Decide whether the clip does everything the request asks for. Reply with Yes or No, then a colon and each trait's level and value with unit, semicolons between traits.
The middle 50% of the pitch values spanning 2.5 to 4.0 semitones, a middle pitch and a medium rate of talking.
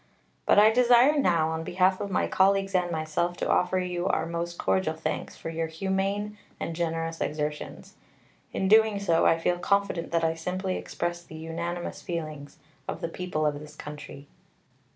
Yes: average, 2.9 semitones; medium, 175 Hz; average, 175 wpm